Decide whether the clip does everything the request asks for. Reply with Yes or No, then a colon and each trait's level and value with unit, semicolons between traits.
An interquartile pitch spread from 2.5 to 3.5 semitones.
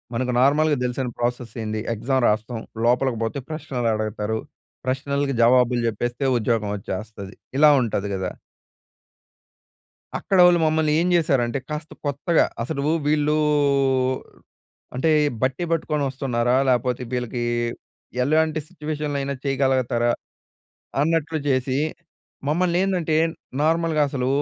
No: average, 4.3 semitones